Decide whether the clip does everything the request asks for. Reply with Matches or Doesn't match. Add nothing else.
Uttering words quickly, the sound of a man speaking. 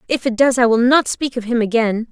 Doesn't match